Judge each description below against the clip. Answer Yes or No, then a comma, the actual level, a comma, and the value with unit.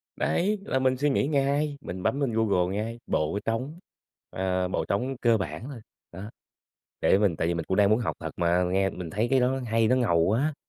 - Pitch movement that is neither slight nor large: No, wide, 6.2 semitones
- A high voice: No, low, 110 Hz